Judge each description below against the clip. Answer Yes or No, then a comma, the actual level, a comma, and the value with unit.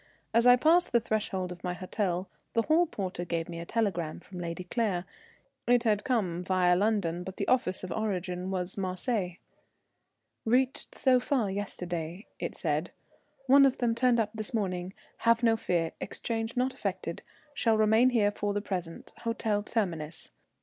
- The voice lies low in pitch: No, high, 205 Hz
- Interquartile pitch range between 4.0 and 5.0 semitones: Yes, average, 4.4 semitones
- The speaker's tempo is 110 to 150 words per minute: No, average, 165 wpm